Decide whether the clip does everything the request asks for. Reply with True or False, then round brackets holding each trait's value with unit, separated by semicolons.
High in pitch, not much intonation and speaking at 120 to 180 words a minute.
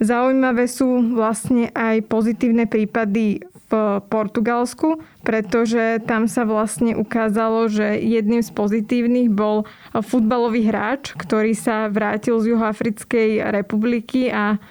False (225 Hz; 1.5 semitones; 110 wpm)